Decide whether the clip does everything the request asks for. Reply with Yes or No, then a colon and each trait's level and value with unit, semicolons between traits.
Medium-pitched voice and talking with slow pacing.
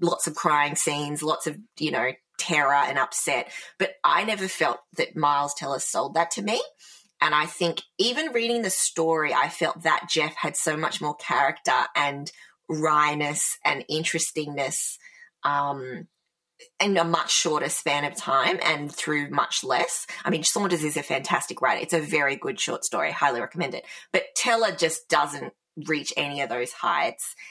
No: medium, 170 Hz; average, 170 wpm